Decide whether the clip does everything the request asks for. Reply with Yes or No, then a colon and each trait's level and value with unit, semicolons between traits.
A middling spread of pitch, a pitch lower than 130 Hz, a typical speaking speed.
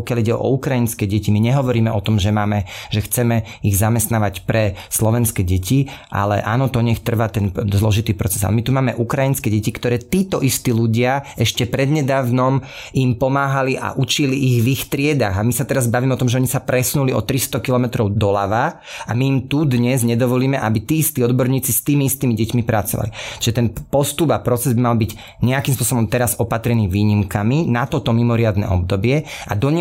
No: average, 3.3 semitones; low, 120 Hz; fast, 190 wpm